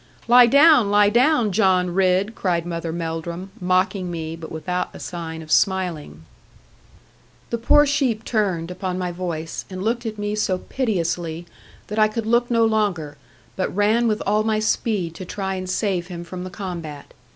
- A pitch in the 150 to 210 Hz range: Yes, medium, 185 Hz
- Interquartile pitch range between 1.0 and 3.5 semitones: No, average, 3.9 semitones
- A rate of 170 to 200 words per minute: Yes, average, 175 wpm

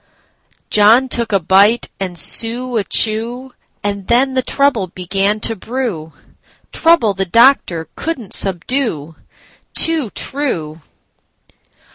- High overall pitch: Yes, high, 220 Hz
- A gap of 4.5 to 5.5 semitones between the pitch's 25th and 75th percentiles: Yes, average, 5.1 semitones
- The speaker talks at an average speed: No, slow, 100 wpm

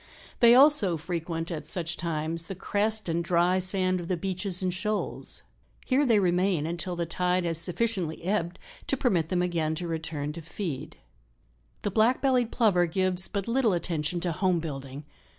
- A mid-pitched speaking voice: Yes, medium, 180 Hz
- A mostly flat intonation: No, average, 3.2 semitones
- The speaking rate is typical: Yes, average, 170 wpm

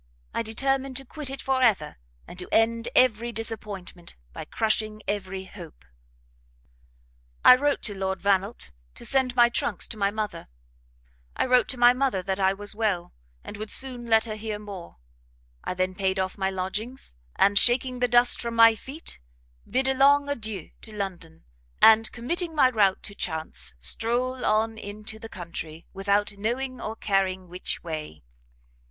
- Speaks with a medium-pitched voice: No, high, 215 Hz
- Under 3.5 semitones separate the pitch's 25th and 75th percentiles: No, average, 4.3 semitones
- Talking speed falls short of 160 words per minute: No, average, 165 wpm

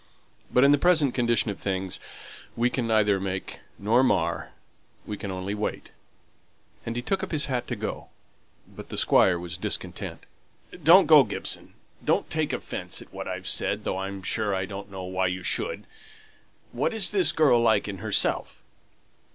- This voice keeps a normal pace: Yes, average, 170 wpm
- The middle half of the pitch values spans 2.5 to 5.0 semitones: No, wide, 5.6 semitones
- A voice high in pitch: No, low, 105 Hz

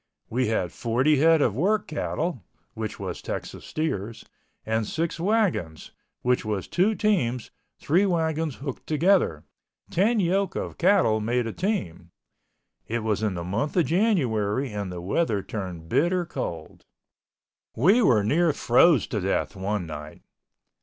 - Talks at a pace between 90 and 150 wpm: Yes, average, 140 wpm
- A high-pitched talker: No, low, 125 Hz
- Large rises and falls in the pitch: Yes, wide, 8.6 semitones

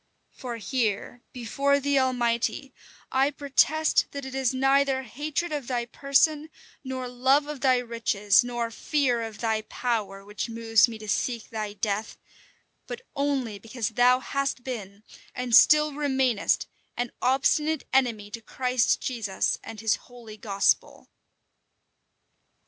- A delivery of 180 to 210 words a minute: No, slow, 135 wpm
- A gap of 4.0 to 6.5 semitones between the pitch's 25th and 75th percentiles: No, average, 3.4 semitones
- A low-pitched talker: No, high, 245 Hz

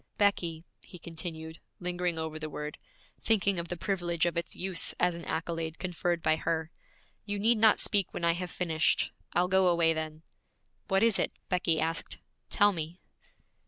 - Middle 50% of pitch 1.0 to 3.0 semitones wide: Yes, narrow, 2.4 semitones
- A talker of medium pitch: Yes, medium, 170 Hz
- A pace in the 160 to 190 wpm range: Yes, average, 170 wpm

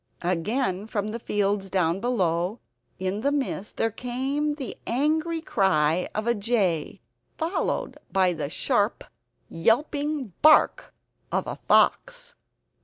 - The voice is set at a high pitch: Yes, high, 220 Hz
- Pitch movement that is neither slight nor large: No, wide, 7.2 semitones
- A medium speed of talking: No, slow, 120 wpm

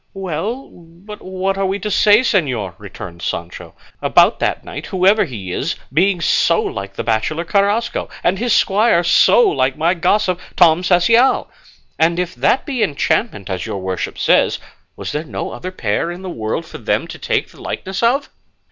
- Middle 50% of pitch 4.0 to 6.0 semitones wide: Yes, wide, 5.5 semitones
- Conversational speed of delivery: Yes, average, 175 wpm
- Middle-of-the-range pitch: Yes, medium, 180 Hz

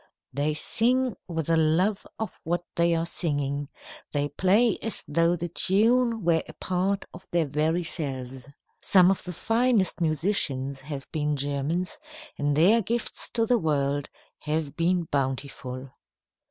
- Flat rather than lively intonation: No, average, 4.8 semitones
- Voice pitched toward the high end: No, medium, 165 Hz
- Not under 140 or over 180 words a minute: Yes, average, 145 wpm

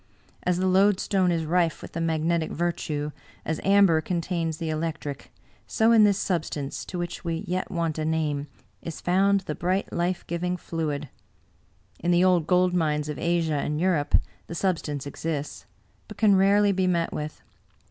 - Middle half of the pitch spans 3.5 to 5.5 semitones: No, average, 2.8 semitones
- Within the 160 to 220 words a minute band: Yes, average, 170 wpm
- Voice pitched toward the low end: No, medium, 170 Hz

